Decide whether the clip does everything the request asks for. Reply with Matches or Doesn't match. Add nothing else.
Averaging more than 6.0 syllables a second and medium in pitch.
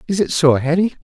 Matches